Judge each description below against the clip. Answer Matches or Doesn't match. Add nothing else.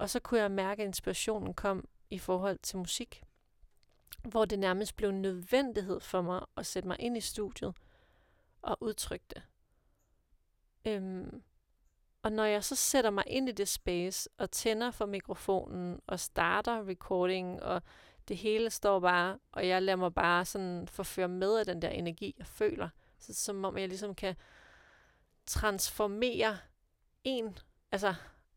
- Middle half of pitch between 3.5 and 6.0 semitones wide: Doesn't match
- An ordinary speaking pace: Matches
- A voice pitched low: Doesn't match